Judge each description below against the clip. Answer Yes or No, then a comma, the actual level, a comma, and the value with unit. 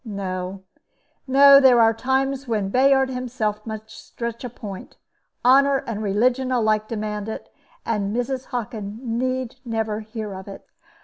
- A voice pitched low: No, high, 230 Hz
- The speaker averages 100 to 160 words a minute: Yes, average, 140 wpm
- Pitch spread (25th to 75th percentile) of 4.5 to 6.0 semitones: No, average, 3.4 semitones